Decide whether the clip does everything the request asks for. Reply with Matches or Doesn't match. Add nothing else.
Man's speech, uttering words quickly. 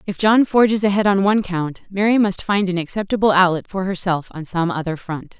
Doesn't match